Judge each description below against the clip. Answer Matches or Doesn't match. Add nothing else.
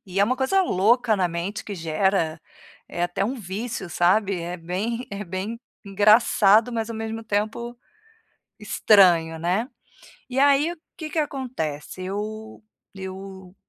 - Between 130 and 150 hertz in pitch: Doesn't match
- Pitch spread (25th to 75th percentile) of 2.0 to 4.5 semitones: Matches